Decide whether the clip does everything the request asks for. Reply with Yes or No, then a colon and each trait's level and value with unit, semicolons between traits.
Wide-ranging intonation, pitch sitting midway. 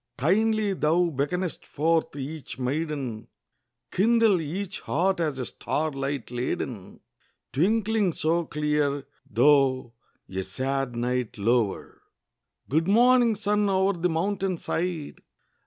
Yes: wide, 6.1 semitones; medium, 155 Hz